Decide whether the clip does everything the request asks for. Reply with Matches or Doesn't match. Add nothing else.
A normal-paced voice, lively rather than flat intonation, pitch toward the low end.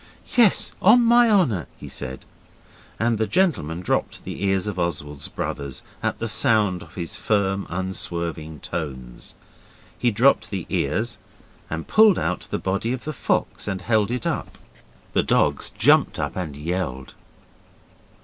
Matches